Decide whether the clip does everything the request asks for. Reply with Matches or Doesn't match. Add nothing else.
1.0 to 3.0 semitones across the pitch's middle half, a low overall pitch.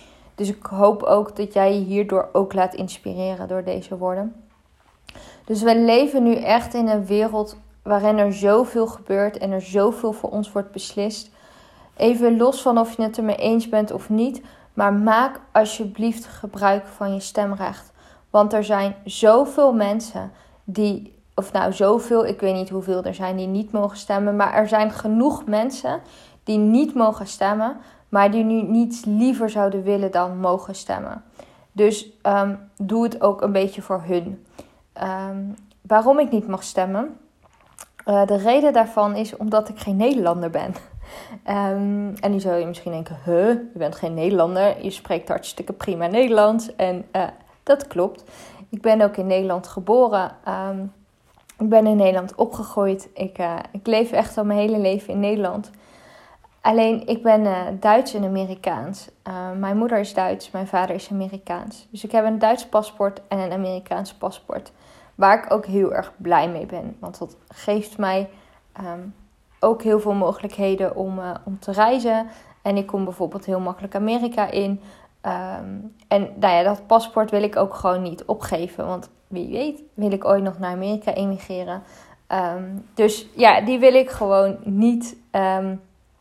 Doesn't match